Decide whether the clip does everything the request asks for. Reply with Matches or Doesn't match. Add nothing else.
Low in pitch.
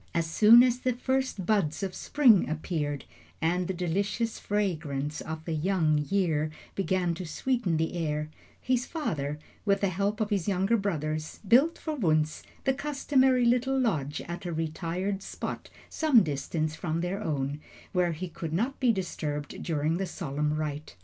Doesn't match